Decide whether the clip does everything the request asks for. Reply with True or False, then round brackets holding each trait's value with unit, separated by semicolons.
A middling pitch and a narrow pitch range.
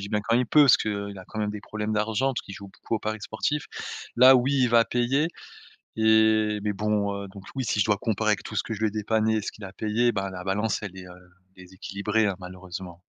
False (105 Hz; 2.0 semitones)